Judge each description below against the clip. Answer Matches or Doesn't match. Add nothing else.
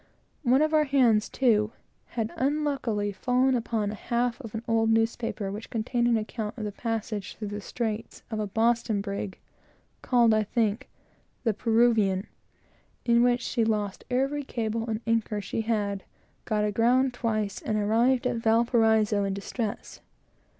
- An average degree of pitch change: Doesn't match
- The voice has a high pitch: Matches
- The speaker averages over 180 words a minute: Doesn't match